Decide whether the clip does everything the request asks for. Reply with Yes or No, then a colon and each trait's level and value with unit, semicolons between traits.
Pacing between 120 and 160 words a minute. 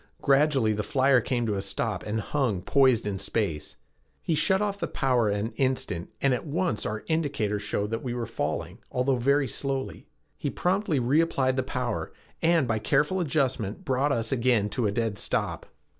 No: average, 180 wpm